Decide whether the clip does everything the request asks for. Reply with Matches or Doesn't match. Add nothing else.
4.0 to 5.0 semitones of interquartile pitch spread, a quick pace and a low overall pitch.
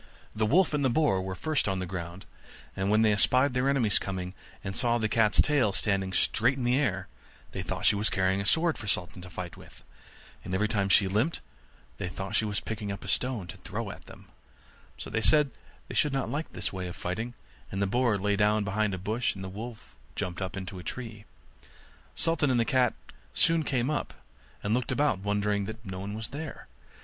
Matches